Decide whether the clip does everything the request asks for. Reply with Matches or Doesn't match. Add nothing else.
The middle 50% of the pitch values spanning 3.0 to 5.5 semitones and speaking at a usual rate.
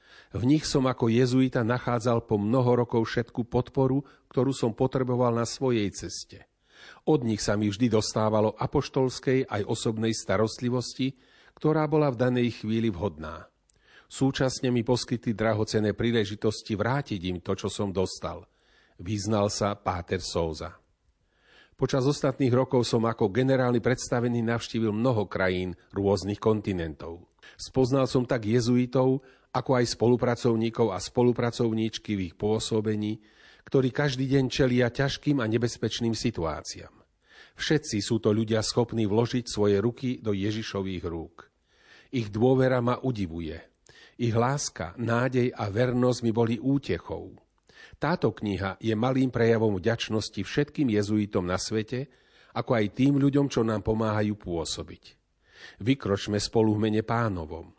Matches